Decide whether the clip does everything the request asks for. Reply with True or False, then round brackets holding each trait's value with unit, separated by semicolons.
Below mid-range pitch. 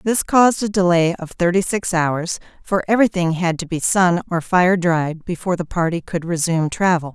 False (175 Hz)